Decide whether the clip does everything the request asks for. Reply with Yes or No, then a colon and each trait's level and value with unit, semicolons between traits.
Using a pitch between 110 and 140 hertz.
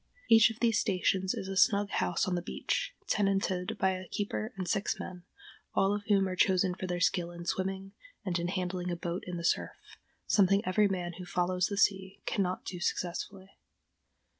No: high, 190 Hz